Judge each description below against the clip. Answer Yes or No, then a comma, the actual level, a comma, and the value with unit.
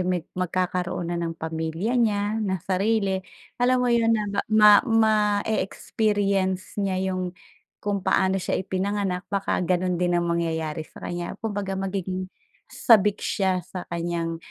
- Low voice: No, high, 190 Hz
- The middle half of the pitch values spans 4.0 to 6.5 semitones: No, average, 2.7 semitones